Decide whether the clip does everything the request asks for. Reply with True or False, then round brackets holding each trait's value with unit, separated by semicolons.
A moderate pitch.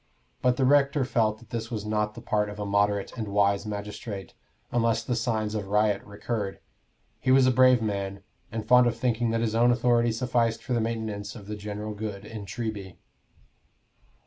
False (110 Hz)